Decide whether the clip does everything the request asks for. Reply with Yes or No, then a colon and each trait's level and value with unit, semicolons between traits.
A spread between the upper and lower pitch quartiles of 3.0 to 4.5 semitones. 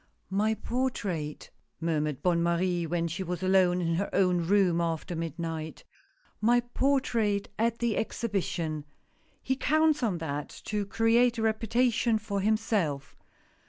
No: average, 5.2 semitones